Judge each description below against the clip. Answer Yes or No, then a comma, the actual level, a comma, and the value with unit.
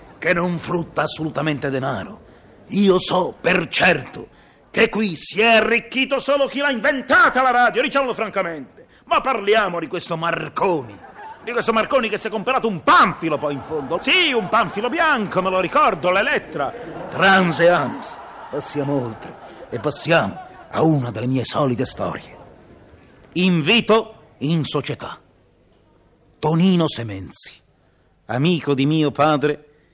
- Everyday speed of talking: Yes, average, 135 wpm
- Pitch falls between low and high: Yes, medium, 175 Hz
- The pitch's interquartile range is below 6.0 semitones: No, wide, 7.2 semitones